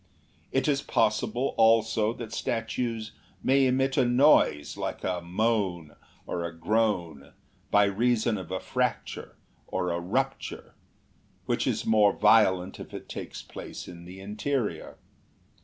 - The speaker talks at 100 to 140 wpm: Yes, slow, 135 wpm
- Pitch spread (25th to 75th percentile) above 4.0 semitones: Yes, average, 4.7 semitones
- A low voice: Yes, low, 110 Hz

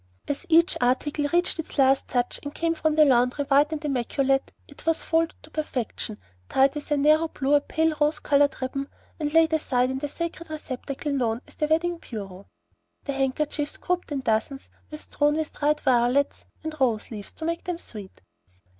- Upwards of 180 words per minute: Yes, average, 190 wpm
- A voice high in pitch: Yes, very high, 290 Hz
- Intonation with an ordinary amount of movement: Yes, average, 3.0 semitones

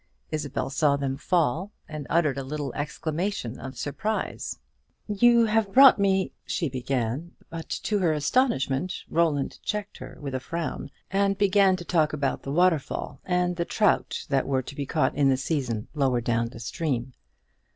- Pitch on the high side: No, medium, 155 Hz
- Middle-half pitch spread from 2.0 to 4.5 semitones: No, wide, 5.6 semitones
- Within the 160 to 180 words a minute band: Yes, average, 170 wpm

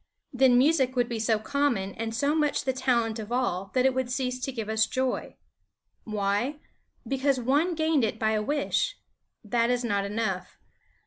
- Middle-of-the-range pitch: No, high, 245 Hz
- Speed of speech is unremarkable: Yes, average, 180 wpm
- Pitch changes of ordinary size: Yes, average, 3.5 semitones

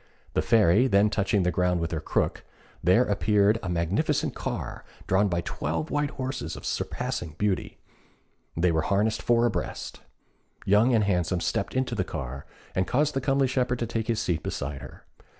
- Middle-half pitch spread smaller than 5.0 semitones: No, wide, 5.4 semitones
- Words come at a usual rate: Yes, average, 175 wpm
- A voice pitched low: Yes, low, 100 Hz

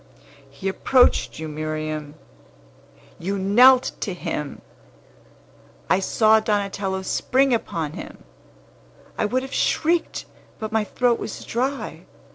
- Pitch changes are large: Yes, wide, 7.0 semitones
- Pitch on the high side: Yes, high, 205 Hz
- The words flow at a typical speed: No, slow, 110 wpm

